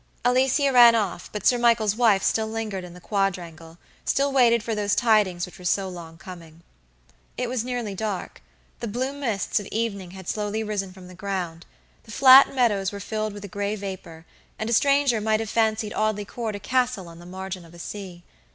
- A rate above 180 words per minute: Yes, average, 200 wpm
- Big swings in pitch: No, average, 3.7 semitones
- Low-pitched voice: No, high, 210 Hz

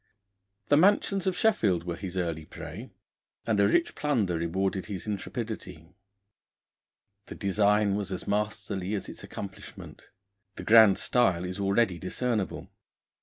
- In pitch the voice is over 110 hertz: No, low, 100 Hz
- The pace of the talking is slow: Yes, slow, 130 wpm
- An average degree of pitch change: Yes, average, 3.4 semitones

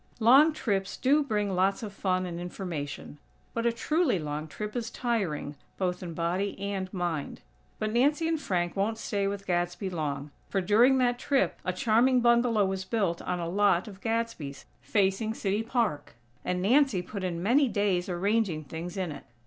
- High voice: Yes, high, 195 Hz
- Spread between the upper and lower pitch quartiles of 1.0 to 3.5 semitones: No, average, 4.6 semitones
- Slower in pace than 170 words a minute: No, average, 175 wpm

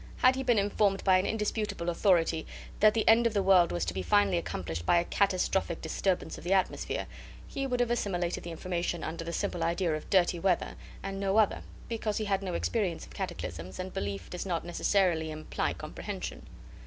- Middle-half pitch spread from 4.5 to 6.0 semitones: No, average, 3.7 semitones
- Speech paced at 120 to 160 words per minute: No, average, 200 wpm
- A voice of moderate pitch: Yes, medium, 180 Hz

